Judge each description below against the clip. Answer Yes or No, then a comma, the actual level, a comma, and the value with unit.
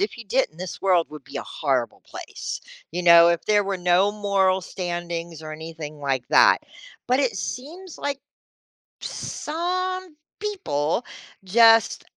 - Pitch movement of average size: No, wide, 7.5 semitones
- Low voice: No, medium, 185 Hz